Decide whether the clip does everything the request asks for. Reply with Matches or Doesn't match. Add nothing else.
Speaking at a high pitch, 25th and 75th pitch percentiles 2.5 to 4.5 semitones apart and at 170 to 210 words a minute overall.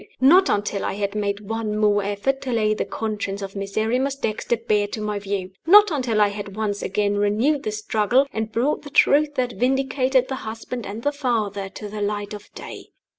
Matches